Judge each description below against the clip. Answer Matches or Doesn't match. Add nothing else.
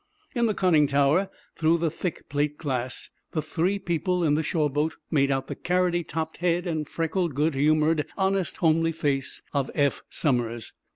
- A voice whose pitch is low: Doesn't match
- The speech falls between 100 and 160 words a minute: Doesn't match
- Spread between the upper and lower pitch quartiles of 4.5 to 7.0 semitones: Doesn't match